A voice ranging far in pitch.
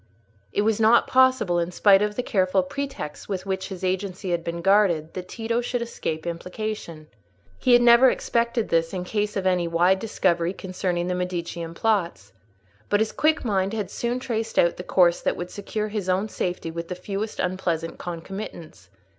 No: average, 3.8 semitones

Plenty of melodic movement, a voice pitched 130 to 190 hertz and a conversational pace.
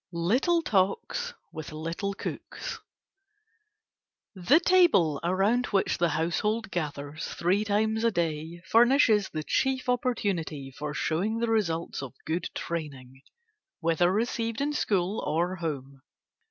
No: wide, 6.0 semitones; medium, 185 Hz; slow, 120 wpm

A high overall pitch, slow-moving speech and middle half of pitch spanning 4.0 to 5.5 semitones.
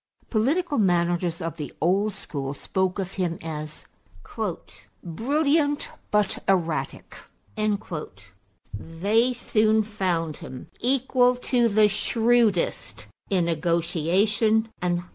Yes: high, 195 Hz; slow, 100 wpm; average, 5.0 semitones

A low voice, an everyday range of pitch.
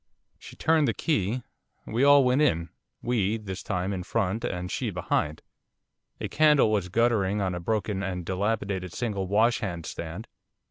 Yes: low, 100 Hz; average, 4.2 semitones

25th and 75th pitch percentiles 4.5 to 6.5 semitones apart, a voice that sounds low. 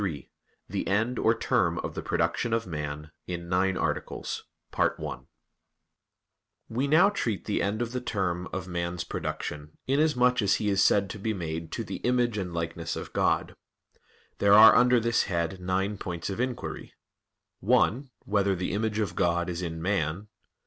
Yes: average, 4.8 semitones; low, 100 Hz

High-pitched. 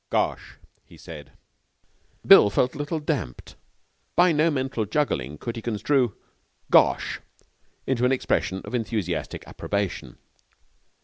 No: low, 120 Hz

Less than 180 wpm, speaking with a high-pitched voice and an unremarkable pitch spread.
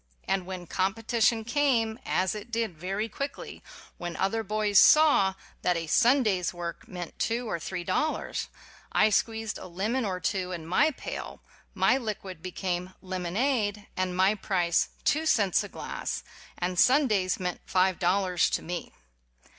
Yes: average, 155 wpm; high, 195 Hz; average, 3.8 semitones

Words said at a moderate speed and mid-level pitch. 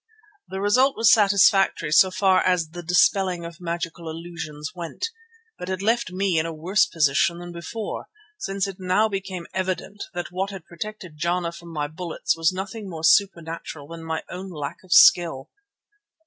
Yes: average, 170 wpm; medium, 180 Hz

